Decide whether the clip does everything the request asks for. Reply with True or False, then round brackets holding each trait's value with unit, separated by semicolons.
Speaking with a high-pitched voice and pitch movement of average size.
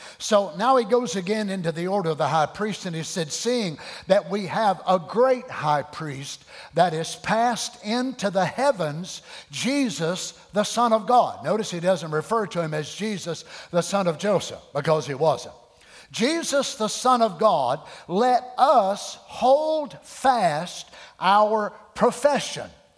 False (200 Hz; 6.1 semitones)